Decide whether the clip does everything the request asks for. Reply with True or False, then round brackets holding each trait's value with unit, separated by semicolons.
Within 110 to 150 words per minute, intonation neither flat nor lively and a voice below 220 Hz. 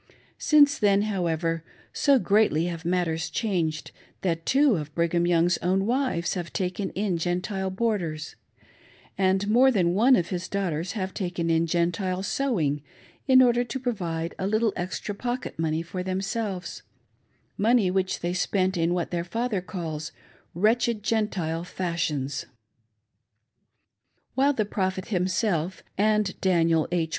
True (140 wpm; 4.0 semitones; 185 Hz)